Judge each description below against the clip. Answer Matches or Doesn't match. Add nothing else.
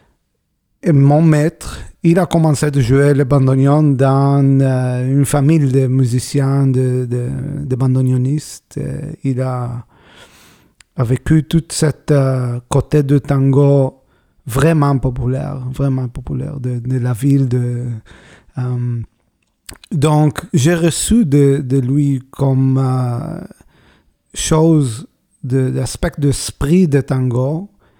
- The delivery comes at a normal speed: Doesn't match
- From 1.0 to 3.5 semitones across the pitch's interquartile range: Matches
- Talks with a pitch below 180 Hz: Matches